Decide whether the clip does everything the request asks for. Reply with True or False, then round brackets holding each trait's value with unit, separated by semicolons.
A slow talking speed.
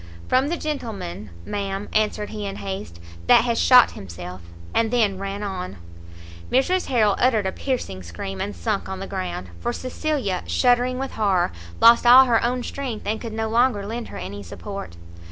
False (175 wpm)